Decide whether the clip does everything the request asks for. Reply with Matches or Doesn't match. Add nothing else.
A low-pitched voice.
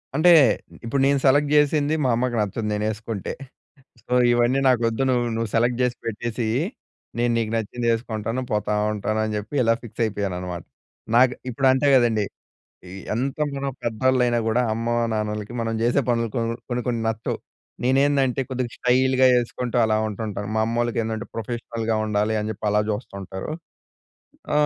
Matches